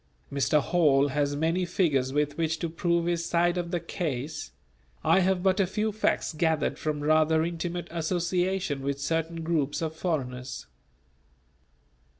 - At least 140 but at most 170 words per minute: Yes, average, 150 wpm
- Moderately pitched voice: Yes, medium, 165 Hz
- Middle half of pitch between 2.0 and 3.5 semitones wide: Yes, average, 3.0 semitones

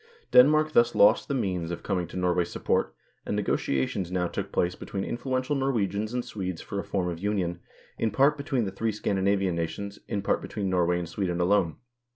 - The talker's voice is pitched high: No, low, 100 Hz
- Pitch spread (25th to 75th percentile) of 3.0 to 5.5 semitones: Yes, average, 4.2 semitones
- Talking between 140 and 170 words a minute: No, average, 190 wpm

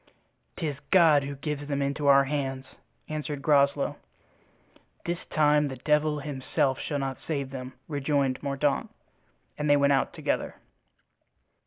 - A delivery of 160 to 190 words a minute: No, slow, 135 wpm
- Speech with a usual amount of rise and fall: No, narrow, 1.5 semitones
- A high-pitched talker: No, medium, 140 Hz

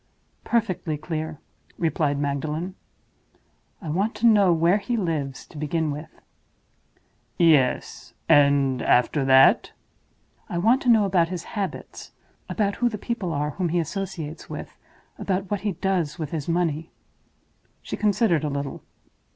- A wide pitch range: No, average, 4.8 semitones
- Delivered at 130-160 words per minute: Yes, average, 140 wpm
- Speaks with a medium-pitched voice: Yes, medium, 165 Hz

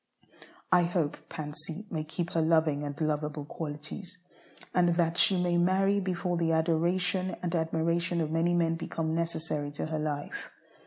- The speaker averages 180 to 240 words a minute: No, average, 155 wpm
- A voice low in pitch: No, medium, 165 Hz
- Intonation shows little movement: Yes, narrow, 2.1 semitones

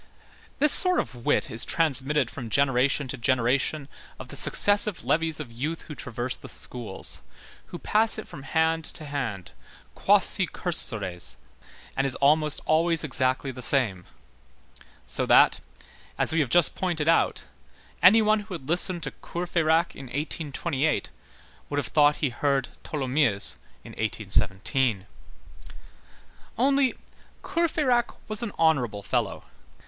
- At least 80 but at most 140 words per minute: Yes, slow, 135 wpm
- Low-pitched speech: No, medium, 145 Hz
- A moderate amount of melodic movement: Yes, average, 4.8 semitones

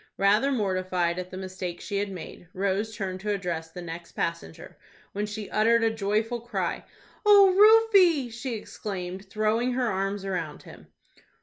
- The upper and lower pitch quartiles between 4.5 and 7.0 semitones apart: No, average, 4.0 semitones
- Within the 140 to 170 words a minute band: Yes, average, 160 wpm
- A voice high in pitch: Yes, high, 205 Hz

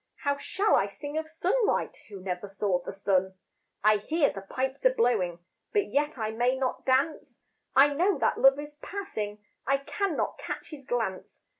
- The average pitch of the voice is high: Yes, very high, 265 Hz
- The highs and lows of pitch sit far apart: Yes, wide, 6.9 semitones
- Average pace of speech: Yes, average, 175 wpm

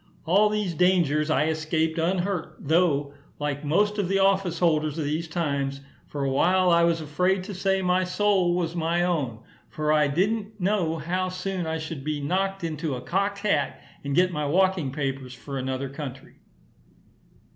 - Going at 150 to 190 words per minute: Yes, average, 175 wpm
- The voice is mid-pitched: Yes, medium, 165 Hz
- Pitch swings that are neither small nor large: Yes, average, 4.0 semitones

